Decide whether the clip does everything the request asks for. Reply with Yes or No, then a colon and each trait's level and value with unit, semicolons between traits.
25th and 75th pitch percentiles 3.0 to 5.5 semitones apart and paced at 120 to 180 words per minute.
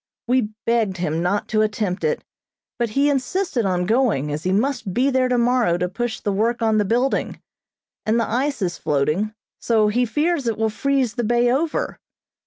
No: average, 3.8 semitones; average, 190 wpm